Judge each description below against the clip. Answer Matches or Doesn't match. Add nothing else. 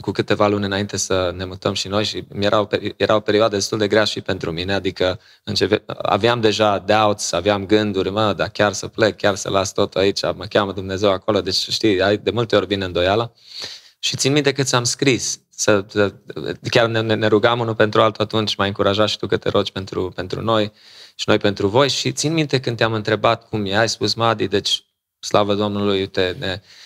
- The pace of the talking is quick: Matches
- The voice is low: Matches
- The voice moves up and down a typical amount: Doesn't match